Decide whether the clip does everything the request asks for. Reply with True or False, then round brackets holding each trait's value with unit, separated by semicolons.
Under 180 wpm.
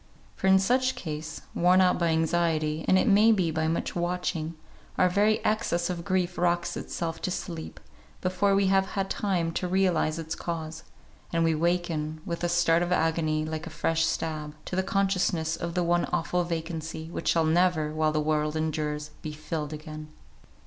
False (185 wpm)